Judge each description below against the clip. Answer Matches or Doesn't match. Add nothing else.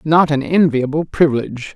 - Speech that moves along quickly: Doesn't match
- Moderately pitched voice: Matches